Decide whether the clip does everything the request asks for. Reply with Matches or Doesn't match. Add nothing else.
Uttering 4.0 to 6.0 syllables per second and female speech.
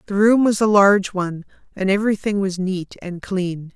Matches